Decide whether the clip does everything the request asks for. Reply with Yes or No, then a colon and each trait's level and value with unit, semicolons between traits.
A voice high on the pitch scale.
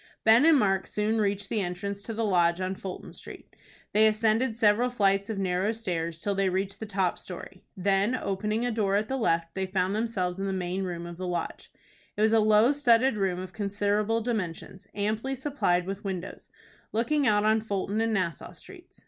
Yes: high, 205 Hz